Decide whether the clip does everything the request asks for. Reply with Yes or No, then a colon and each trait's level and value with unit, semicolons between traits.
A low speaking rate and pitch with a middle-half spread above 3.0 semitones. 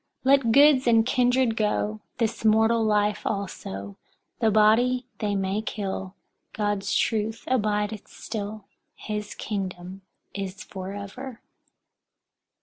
No: slow, 105 wpm; narrow, 2.4 semitones